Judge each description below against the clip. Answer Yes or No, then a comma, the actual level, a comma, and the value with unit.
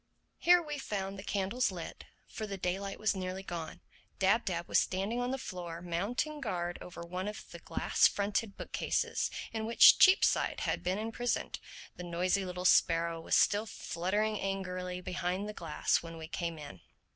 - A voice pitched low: No, high, 190 Hz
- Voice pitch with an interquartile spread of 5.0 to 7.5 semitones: No, average, 3.2 semitones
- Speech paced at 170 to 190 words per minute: Yes, average, 175 wpm